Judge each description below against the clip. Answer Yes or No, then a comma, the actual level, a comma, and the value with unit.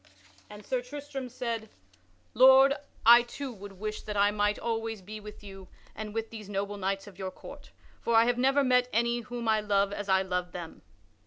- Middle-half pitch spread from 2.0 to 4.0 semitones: Yes, average, 3.1 semitones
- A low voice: No, high, 215 Hz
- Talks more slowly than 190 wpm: No, average, 195 wpm